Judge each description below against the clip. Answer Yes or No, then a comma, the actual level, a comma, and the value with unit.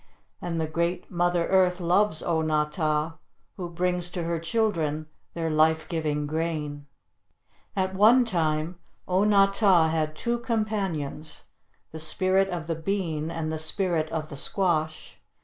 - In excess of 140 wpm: Yes, average, 150 wpm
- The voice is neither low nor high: Yes, medium, 170 Hz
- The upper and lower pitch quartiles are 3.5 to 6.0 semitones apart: No, average, 3.1 semitones